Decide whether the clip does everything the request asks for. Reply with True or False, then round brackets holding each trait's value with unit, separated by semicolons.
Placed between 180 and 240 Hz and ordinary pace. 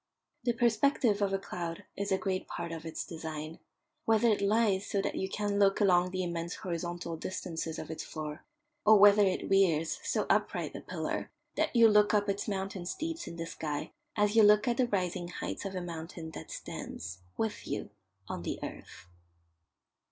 True (190 Hz; 190 wpm)